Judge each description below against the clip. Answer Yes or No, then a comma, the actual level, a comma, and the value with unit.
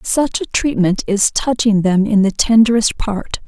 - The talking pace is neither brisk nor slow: Yes, average, 175 wpm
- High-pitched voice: Yes, high, 220 Hz